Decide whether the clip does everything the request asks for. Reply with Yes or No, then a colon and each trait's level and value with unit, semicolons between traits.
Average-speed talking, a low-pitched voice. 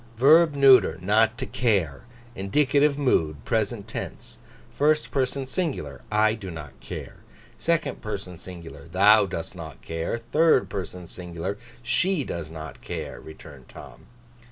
No: slow, 130 wpm; low, 105 Hz